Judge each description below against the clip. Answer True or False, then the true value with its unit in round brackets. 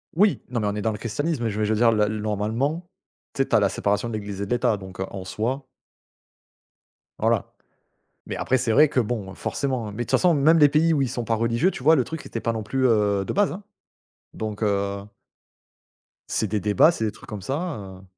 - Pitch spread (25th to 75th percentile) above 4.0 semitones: True (4.9 semitones)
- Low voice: True (115 Hz)